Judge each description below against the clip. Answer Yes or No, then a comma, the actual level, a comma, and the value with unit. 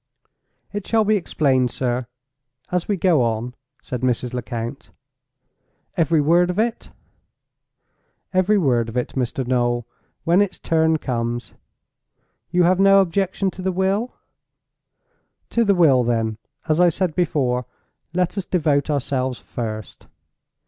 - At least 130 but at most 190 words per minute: Yes, slow, 135 wpm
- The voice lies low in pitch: No, medium, 155 Hz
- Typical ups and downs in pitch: No, wide, 7.0 semitones